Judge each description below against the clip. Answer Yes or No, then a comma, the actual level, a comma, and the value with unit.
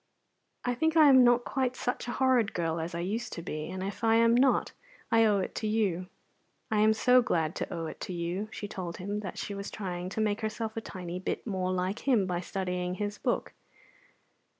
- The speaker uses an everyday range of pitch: Yes, average, 4.1 semitones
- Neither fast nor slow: No, fast, 220 wpm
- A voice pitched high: Yes, high, 205 Hz